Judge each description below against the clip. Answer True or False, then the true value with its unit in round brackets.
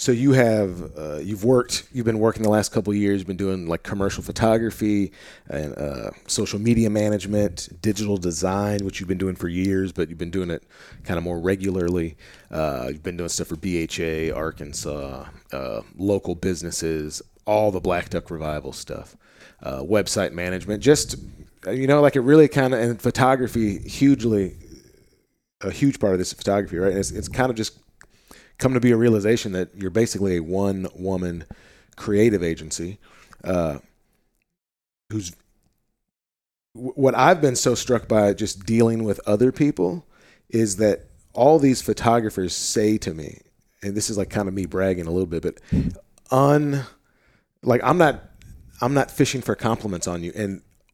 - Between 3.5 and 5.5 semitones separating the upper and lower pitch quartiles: True (4.4 semitones)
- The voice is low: True (100 Hz)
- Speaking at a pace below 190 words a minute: True (170 wpm)